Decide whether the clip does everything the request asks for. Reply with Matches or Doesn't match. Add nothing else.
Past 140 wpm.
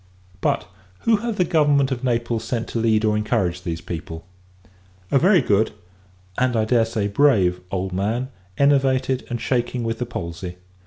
Matches